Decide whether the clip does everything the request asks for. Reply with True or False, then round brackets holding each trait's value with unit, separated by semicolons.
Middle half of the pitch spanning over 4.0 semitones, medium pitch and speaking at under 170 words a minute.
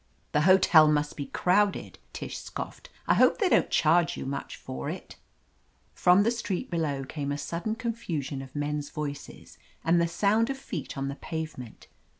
False (5.5 semitones; 160 Hz; 175 wpm)